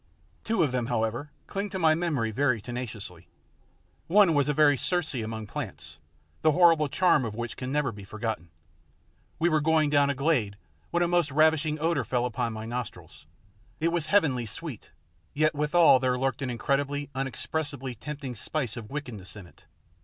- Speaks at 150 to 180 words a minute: Yes, average, 175 wpm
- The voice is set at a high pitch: No, medium, 140 Hz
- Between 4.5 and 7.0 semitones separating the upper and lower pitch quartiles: Yes, average, 5.1 semitones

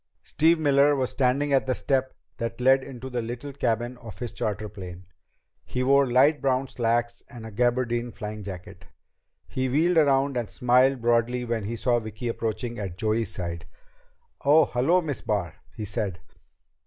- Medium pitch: No, low, 120 Hz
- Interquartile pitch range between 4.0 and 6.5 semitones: No, average, 3.2 semitones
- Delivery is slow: No, average, 165 wpm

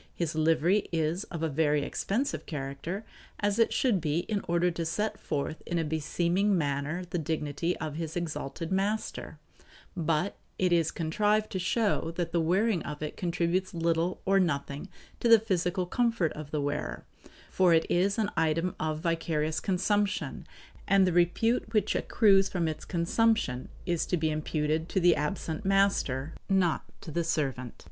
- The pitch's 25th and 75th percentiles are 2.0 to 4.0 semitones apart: Yes, average, 3.7 semitones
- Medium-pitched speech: Yes, medium, 170 Hz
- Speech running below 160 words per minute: No, average, 165 wpm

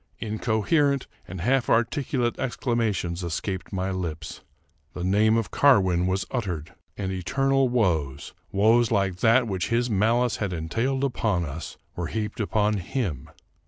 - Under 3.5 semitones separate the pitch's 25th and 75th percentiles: No, average, 4.9 semitones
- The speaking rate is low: No, average, 155 wpm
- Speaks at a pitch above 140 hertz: No, low, 105 Hz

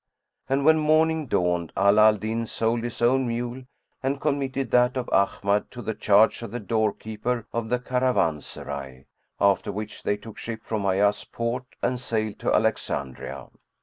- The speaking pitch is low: Yes, low, 115 Hz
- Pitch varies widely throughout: No, average, 3.5 semitones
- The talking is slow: No, average, 165 wpm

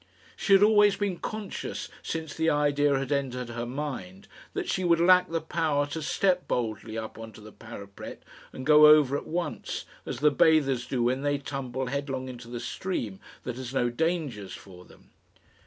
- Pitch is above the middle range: No, medium, 140 Hz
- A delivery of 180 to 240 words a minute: Yes, average, 185 wpm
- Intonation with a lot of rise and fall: No, average, 5.0 semitones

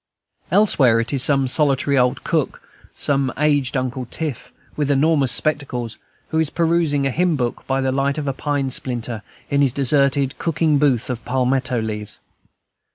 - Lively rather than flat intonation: No, average, 2.7 semitones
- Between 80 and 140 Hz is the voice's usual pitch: Yes, low, 135 Hz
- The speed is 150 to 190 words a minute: Yes, average, 160 wpm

